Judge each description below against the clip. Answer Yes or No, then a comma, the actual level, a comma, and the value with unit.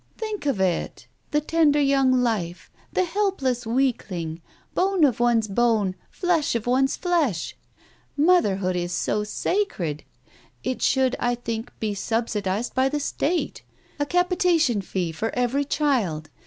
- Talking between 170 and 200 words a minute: No, average, 140 wpm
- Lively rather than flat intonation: Yes, wide, 6.5 semitones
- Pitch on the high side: Yes, high, 245 Hz